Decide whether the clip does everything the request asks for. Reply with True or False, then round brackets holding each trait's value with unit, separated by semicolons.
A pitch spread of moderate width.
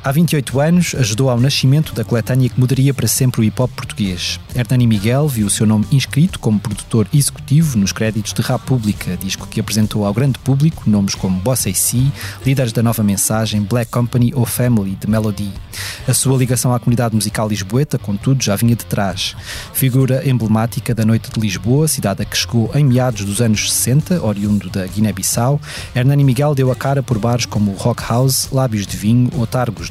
True (4.0 semitones)